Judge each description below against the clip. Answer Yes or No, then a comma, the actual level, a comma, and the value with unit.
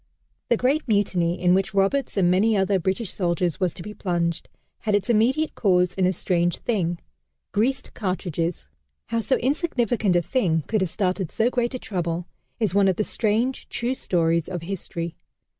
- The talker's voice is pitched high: Yes, high, 195 Hz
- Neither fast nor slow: Yes, average, 175 wpm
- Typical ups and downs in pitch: Yes, average, 4.4 semitones